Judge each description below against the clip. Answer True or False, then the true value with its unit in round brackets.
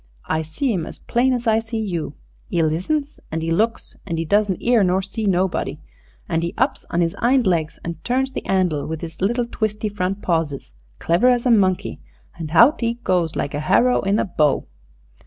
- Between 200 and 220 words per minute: True (205 wpm)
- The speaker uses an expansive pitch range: True (5.9 semitones)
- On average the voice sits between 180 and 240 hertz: True (190 Hz)